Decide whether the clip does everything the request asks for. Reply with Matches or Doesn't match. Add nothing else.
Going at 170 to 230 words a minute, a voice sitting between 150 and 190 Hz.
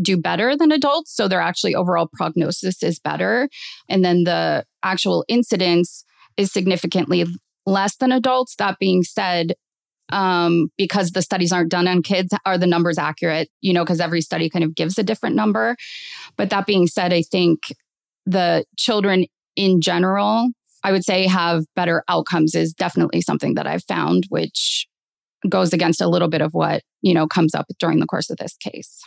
Matches